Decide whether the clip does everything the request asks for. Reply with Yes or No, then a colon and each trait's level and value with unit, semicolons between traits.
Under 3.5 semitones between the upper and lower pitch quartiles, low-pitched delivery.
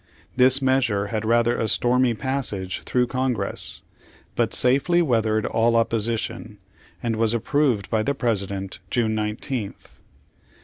Yes: average, 3.0 semitones; low, 115 Hz